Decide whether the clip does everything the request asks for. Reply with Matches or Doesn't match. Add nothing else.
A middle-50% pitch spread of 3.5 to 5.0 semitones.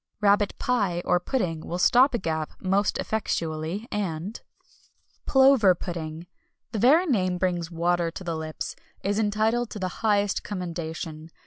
Matches